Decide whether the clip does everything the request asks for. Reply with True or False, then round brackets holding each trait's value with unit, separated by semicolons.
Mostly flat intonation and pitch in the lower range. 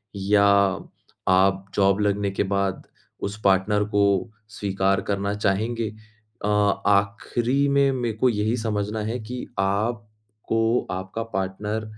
True (2.2 semitones; 105 Hz)